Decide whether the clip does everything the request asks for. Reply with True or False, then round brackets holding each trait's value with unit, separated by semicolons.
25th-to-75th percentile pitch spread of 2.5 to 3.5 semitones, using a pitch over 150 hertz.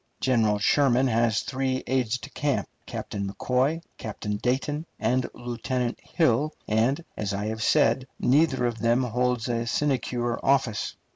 False (2.8 semitones; 125 Hz)